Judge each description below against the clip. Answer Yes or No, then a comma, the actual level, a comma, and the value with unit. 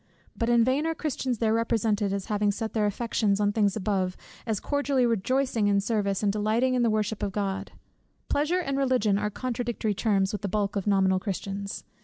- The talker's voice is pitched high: Yes, high, 215 Hz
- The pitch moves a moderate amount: Yes, average, 3.2 semitones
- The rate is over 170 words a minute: Yes, average, 200 wpm